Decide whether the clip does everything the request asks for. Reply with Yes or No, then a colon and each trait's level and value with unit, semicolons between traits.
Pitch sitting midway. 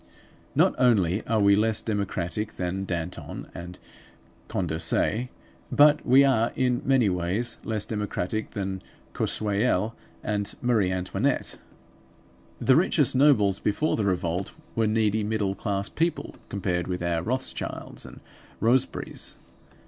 No: low, 105 Hz